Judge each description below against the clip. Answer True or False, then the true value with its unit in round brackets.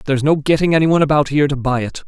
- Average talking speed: False (290 wpm)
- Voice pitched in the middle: True (145 Hz)